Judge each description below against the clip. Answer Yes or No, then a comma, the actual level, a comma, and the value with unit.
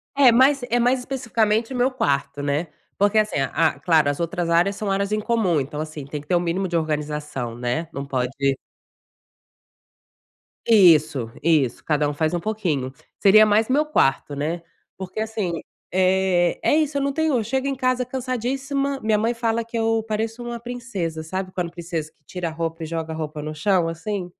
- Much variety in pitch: Yes, wide, 6.8 semitones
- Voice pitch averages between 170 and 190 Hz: Yes, medium, 185 Hz